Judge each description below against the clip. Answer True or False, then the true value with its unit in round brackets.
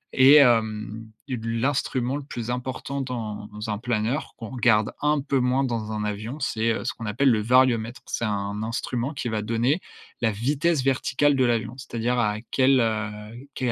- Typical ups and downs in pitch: True (3.2 semitones)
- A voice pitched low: True (120 Hz)